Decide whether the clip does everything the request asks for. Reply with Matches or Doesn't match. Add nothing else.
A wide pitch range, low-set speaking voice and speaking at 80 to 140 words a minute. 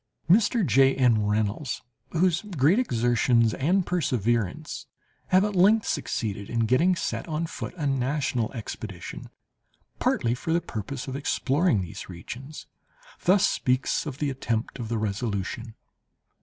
Matches